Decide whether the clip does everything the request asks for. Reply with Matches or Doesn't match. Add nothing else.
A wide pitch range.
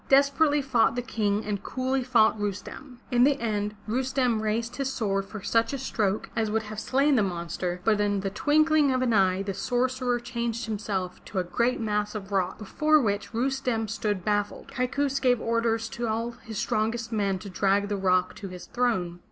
Doesn't match